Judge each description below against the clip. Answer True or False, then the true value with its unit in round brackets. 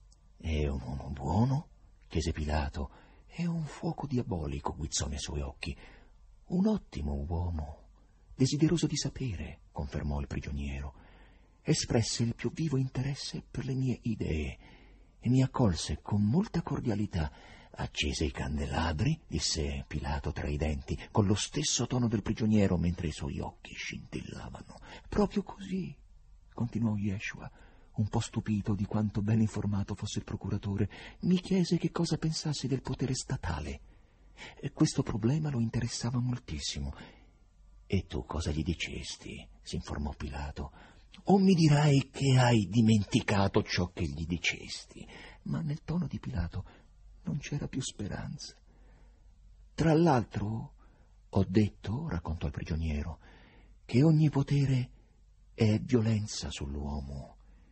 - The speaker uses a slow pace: False (130 wpm)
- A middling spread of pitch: False (8.3 semitones)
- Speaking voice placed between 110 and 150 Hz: False (100 Hz)